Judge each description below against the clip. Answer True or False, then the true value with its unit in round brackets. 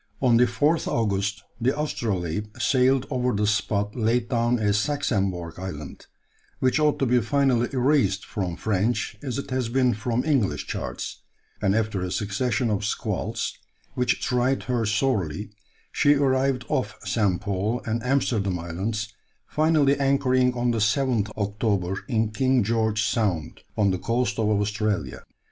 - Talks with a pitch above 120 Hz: False (115 Hz)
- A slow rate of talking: False (150 wpm)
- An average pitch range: True (4.0 semitones)